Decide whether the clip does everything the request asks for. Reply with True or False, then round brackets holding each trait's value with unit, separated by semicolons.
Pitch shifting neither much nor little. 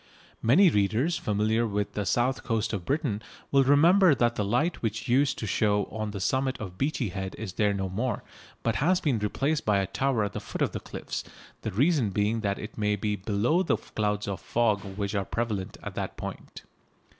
True (4.6 semitones)